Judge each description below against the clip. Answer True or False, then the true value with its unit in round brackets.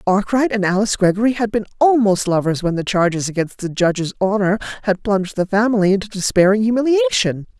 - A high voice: True (200 Hz)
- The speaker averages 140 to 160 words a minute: False (175 wpm)